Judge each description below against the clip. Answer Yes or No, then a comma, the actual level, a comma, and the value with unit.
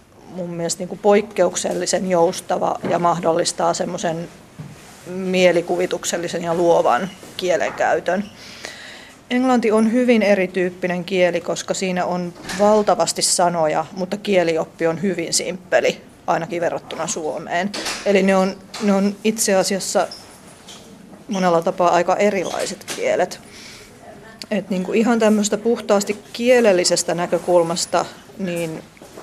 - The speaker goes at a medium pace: Yes, average, 105 wpm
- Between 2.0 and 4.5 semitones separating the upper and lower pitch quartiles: Yes, average, 2.9 semitones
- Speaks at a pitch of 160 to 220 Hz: Yes, medium, 185 Hz